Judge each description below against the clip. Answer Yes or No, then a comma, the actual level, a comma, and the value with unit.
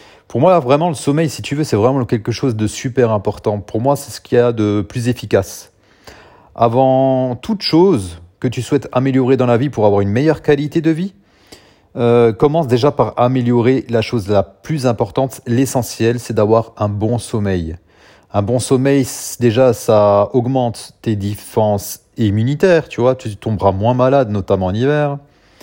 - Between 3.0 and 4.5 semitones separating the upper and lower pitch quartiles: Yes, average, 4.2 semitones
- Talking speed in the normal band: Yes, average, 180 wpm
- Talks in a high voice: No, low, 120 Hz